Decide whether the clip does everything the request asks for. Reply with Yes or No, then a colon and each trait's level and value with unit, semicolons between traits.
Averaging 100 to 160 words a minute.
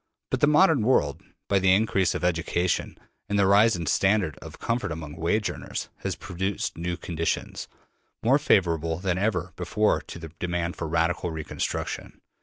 No: average, 170 wpm